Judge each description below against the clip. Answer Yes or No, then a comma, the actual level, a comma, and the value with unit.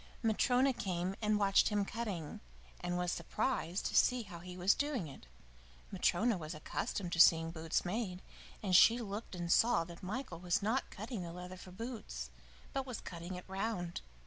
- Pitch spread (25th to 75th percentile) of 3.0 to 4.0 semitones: No, average, 4.4 semitones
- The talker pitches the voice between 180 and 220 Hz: Yes, medium, 185 Hz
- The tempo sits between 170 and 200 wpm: Yes, average, 175 wpm